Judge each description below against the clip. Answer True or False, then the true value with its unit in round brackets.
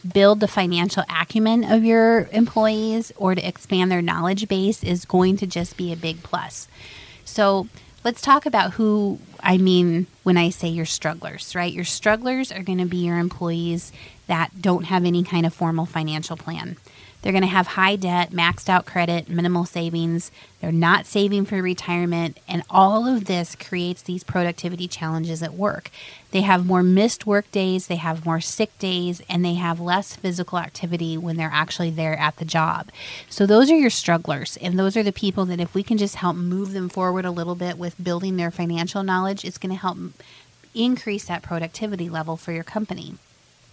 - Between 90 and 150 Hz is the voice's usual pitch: False (180 Hz)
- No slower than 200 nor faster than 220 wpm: False (190 wpm)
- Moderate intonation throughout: False (2.3 semitones)